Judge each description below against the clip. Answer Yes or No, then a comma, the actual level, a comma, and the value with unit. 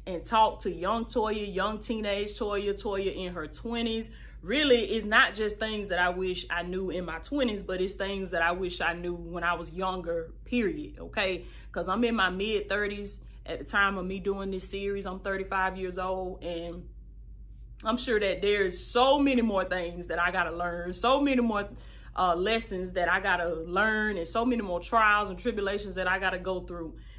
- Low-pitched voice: No, high, 195 Hz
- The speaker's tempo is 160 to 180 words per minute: No, average, 200 wpm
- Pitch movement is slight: No, average, 3.1 semitones